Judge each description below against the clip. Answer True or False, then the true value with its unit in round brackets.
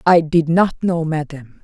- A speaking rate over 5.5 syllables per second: False (4.2 syllables/s)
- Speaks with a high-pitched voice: False (160 Hz)